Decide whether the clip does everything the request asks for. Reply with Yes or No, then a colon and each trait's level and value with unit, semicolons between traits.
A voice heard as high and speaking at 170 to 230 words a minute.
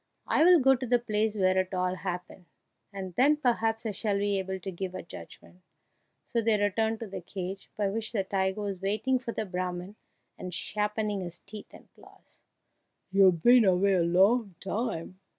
Yes: high, 200 Hz; average, 185 wpm